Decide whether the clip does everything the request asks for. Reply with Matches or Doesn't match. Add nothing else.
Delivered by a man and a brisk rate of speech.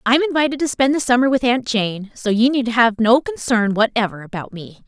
Doesn't match